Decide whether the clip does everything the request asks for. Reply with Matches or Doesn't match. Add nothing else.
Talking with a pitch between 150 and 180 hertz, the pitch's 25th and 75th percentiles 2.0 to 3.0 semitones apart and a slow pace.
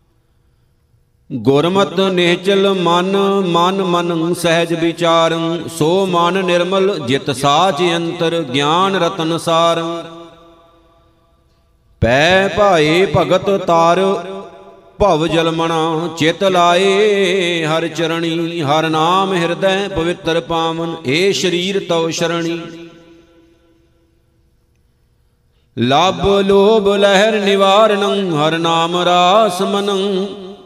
Matches